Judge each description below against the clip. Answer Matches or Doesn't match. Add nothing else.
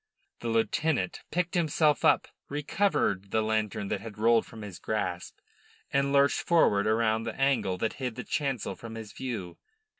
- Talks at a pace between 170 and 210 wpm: Doesn't match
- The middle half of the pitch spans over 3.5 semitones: Matches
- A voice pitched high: Doesn't match